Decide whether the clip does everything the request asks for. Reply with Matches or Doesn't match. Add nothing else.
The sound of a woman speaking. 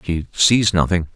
Doesn't match